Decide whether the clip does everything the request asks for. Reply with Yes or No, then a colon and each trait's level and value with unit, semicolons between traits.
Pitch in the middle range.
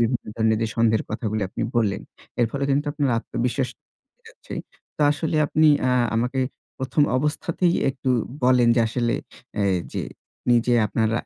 No: low, 125 Hz